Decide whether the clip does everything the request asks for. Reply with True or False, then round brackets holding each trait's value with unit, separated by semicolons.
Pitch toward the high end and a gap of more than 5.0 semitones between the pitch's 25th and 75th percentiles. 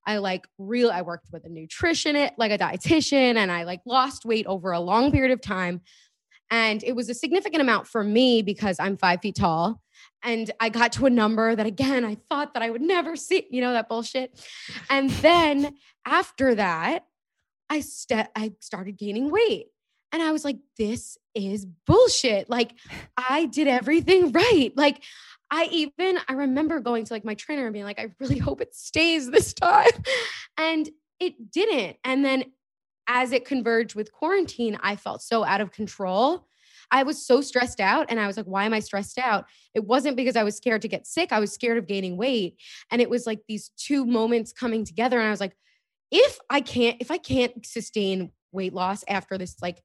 True (240 Hz; 5.4 semitones)